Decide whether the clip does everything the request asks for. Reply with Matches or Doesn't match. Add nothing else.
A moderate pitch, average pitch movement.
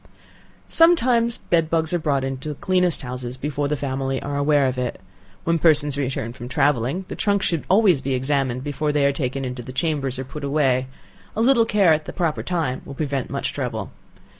Matches